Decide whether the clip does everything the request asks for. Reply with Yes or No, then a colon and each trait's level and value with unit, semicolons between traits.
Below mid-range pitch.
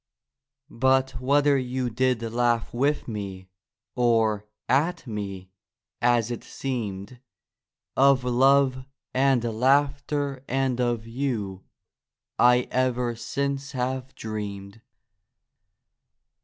Yes: low, 125 Hz